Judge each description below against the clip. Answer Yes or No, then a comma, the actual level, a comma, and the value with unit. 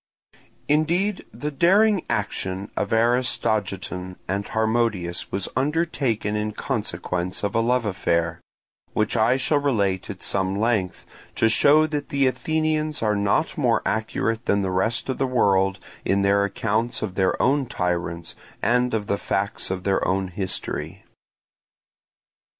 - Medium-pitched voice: No, low, 110 Hz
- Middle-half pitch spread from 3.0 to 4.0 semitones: No, average, 5.2 semitones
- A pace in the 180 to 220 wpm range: No, average, 140 wpm